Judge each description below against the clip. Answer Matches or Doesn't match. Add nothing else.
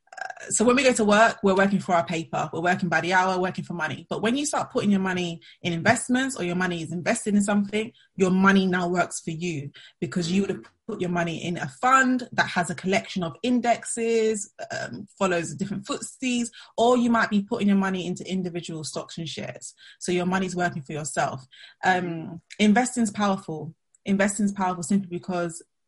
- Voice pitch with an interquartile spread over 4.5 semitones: Doesn't match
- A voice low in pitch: Doesn't match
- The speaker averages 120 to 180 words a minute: Doesn't match